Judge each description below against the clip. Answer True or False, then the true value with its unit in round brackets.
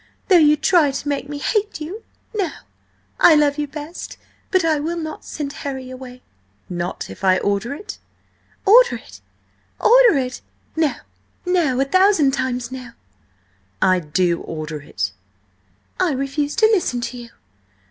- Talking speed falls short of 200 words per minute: True (155 wpm)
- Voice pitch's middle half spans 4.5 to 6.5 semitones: True (5.2 semitones)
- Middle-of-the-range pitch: False (285 Hz)